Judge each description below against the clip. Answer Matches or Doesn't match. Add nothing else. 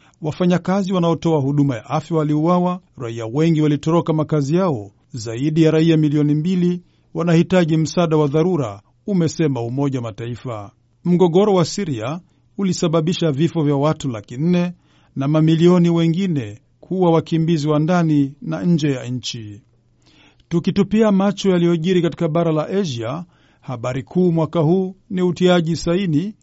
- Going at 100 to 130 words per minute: Matches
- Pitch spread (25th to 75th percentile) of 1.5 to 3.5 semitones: Doesn't match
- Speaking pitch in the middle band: Matches